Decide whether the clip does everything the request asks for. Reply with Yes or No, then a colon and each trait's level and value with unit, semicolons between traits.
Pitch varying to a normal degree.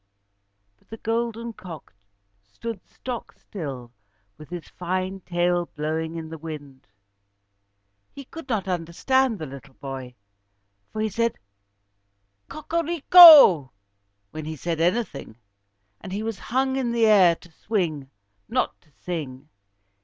No: wide, 6.9 semitones